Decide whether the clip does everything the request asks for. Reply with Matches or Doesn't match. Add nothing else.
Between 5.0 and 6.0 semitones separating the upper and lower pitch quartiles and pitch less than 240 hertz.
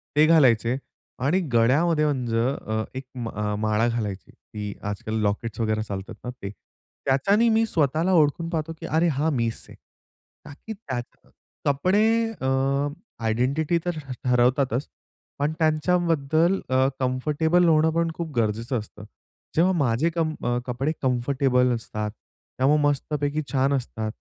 Matches